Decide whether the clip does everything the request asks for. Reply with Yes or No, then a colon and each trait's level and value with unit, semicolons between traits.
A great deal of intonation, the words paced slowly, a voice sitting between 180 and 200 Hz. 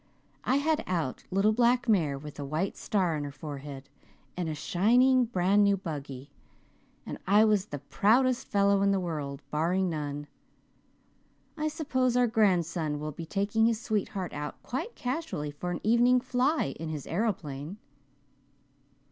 No: wide, 7.5 semitones; average, 155 wpm; high, 190 Hz